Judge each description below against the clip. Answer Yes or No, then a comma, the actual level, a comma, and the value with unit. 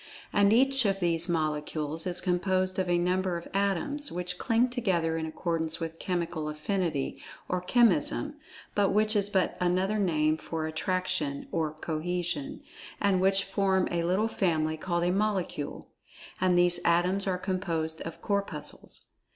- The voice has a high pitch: No, medium, 180 Hz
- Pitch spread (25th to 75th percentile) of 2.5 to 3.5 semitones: Yes, average, 3.2 semitones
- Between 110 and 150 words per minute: Yes, average, 145 wpm